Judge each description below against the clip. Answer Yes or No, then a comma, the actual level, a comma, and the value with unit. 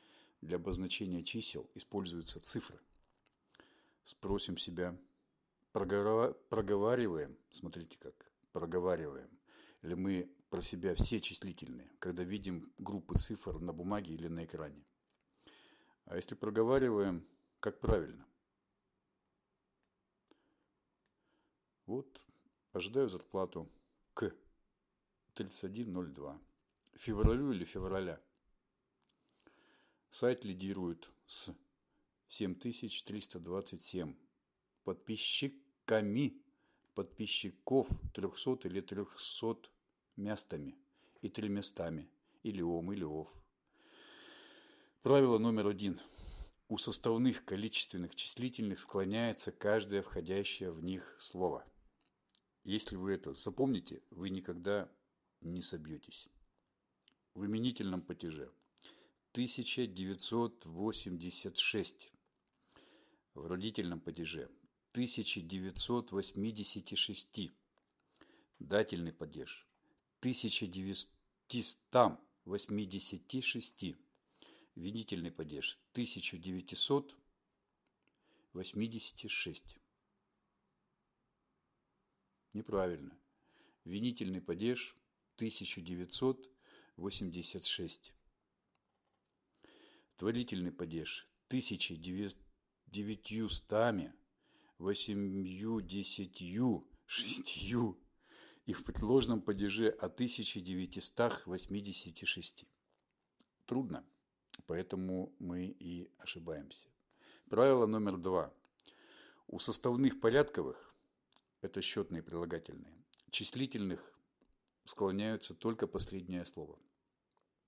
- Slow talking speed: Yes, slow, 65 wpm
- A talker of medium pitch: No, low, 100 Hz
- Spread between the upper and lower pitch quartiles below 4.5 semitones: Yes, average, 3.6 semitones